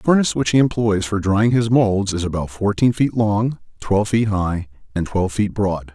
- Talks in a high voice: No, low, 105 Hz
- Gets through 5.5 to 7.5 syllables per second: No, 5.2 syllables/s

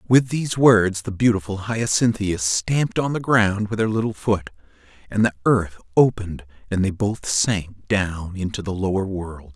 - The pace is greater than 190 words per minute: No, average, 170 wpm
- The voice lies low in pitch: Yes, low, 100 Hz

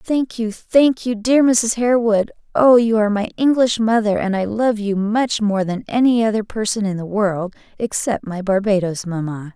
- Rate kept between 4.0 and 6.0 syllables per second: Yes, 4.8 syllables/s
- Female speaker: Yes, female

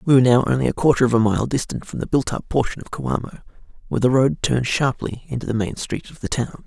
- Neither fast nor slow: No, fast, 260 wpm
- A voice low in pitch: Yes, low, 125 Hz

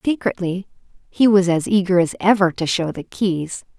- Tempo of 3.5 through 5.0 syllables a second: Yes, 4.9 syllables/s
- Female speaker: Yes, female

